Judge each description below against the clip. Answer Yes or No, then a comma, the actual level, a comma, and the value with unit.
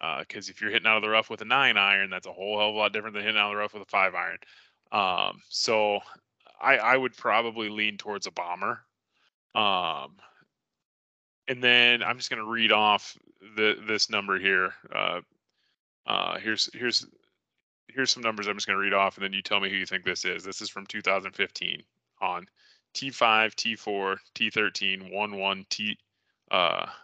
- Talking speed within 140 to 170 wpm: No, average, 190 wpm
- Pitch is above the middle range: No, low, 105 Hz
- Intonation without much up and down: Yes, narrow, 2.0 semitones